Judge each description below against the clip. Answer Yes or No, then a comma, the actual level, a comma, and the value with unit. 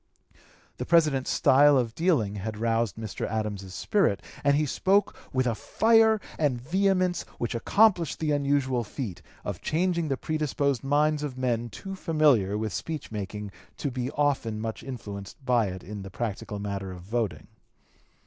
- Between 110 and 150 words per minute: No, average, 160 wpm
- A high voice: No, low, 130 Hz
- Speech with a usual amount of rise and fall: No, wide, 6.2 semitones